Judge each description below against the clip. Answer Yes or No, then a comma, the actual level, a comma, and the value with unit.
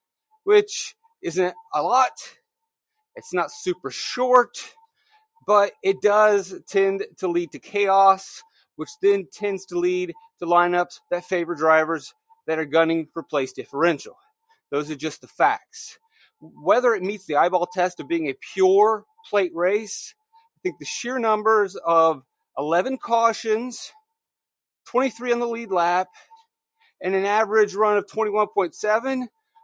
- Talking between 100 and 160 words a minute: Yes, average, 140 wpm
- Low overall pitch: No, high, 215 Hz